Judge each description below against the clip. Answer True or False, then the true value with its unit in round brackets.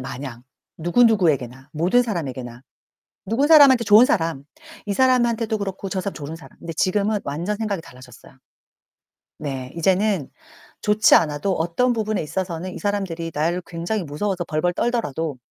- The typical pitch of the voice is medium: True (180 Hz)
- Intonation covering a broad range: True (5.7 semitones)